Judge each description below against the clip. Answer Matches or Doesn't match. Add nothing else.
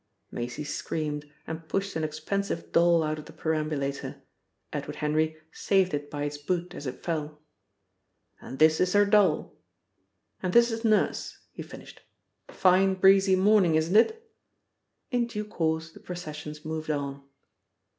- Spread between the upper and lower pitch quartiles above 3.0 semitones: Matches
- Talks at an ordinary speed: Matches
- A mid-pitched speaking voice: Matches